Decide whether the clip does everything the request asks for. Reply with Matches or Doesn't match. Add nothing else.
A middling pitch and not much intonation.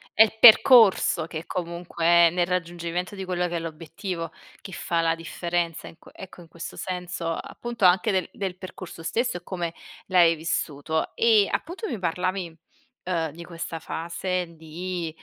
Matches